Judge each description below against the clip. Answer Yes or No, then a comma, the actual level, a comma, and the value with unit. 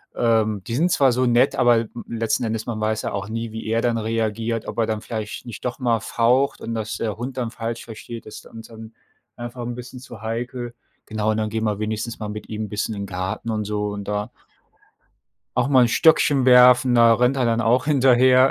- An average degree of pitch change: No, narrow, 2.1 semitones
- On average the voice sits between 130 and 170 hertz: No, low, 115 Hz